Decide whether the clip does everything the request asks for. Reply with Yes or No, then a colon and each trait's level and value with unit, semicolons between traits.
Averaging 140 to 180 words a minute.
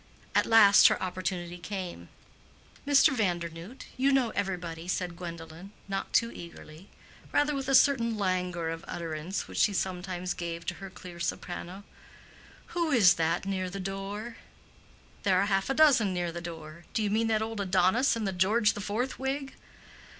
Yes: average, 165 wpm